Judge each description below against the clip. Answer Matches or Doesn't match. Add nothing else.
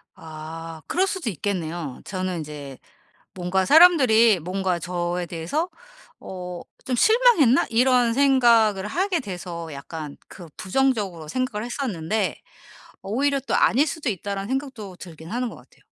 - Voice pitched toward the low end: Doesn't match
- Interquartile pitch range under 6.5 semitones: Doesn't match